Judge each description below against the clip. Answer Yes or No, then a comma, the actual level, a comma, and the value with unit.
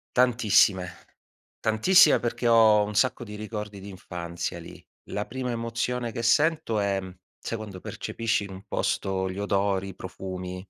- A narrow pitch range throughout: No, average, 3.5 semitones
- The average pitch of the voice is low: Yes, low, 105 Hz